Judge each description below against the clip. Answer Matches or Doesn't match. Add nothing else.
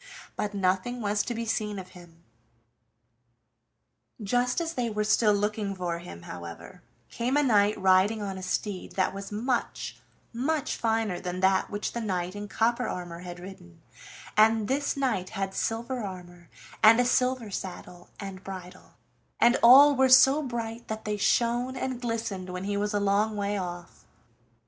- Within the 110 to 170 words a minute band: Matches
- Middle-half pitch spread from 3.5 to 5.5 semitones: Matches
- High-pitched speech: Matches